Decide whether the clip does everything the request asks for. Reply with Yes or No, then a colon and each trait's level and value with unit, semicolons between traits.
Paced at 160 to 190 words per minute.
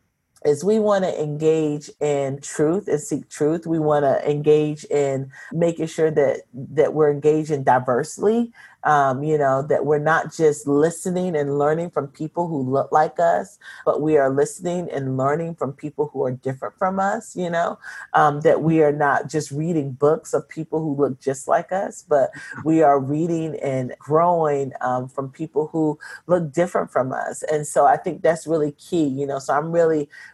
Yes: average, 185 wpm